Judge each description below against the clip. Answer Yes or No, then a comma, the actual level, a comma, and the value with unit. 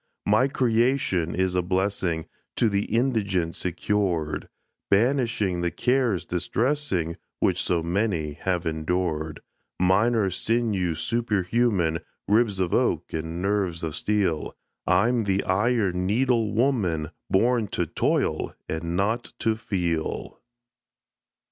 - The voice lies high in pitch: No, very low, 95 Hz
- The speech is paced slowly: Yes, slow, 115 wpm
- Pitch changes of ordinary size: Yes, average, 4.7 semitones